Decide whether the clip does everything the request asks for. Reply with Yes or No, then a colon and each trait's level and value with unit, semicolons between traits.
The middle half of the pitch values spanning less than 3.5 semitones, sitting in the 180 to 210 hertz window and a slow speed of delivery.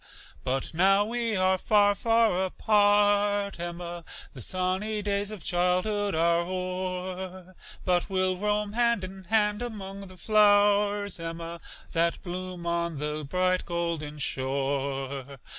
Yes: average, 3.1 semitones; medium, 185 Hz; slow, 125 wpm